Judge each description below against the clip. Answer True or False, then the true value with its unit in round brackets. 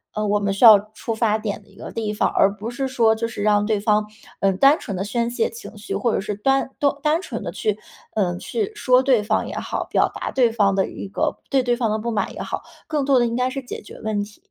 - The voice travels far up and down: False (3.4 semitones)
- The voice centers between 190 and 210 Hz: False (220 Hz)